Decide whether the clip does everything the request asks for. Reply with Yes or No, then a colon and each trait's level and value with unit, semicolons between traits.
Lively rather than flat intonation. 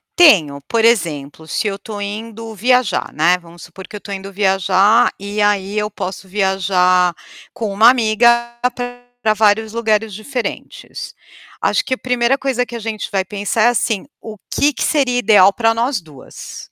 No: average, 3.6 semitones